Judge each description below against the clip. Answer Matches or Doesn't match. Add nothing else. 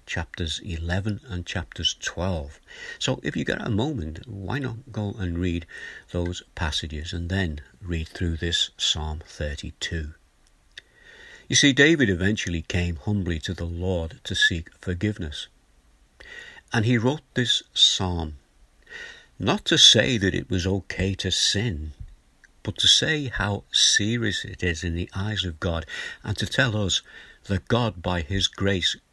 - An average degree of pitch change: Matches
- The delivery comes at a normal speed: Matches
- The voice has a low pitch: Matches